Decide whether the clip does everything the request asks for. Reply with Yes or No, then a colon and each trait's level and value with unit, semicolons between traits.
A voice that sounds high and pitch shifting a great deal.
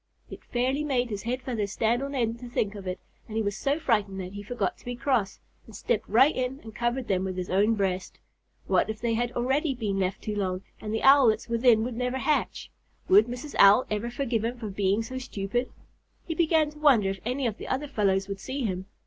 No: high, 230 Hz; average, 4.2 semitones